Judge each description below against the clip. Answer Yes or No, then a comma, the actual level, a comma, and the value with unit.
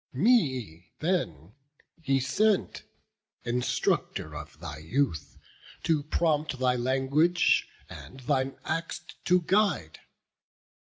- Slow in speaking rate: Yes, slow, 95 wpm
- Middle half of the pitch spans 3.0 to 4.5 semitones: No, wide, 5.5 semitones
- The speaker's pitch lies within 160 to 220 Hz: No, low, 135 Hz